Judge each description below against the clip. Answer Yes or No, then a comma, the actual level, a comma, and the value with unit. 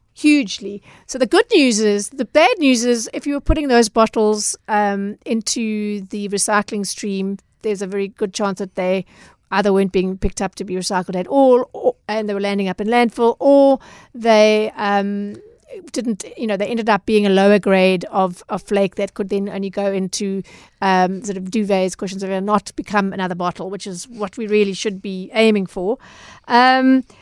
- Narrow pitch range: No, average, 3.1 semitones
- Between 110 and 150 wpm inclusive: No, average, 195 wpm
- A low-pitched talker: No, high, 205 Hz